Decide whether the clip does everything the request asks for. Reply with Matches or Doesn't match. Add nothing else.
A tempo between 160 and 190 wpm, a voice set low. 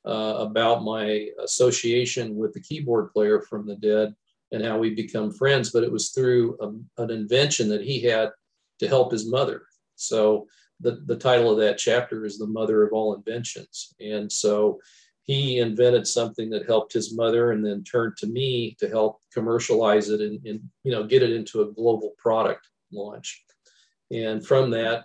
Matches